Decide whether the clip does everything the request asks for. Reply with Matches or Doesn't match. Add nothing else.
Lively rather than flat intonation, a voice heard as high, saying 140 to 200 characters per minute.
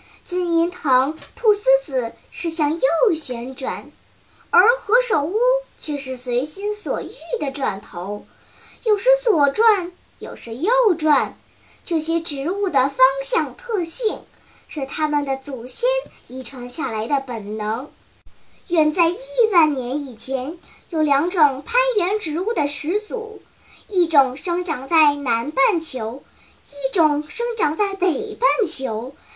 Matches